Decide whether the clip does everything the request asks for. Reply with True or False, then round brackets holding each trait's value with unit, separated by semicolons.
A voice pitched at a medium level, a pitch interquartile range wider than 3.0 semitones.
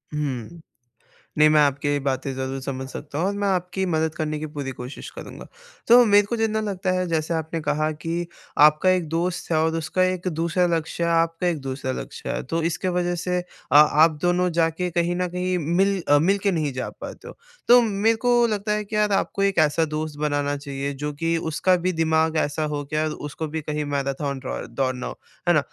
True (165 Hz; 3.6 semitones)